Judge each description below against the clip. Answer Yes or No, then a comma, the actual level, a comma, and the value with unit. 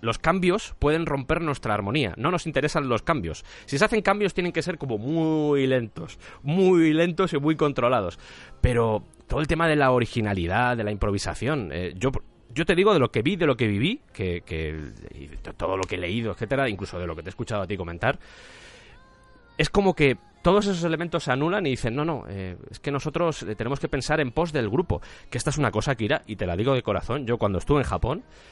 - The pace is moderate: No, fast, 225 wpm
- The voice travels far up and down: Yes, wide, 7.5 semitones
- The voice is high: No, low, 130 Hz